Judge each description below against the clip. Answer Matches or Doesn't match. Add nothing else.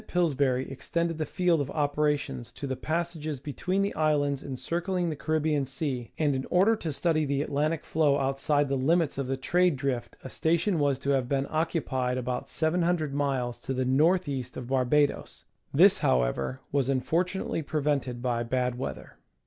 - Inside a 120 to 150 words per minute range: Doesn't match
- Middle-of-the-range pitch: Matches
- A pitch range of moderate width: Matches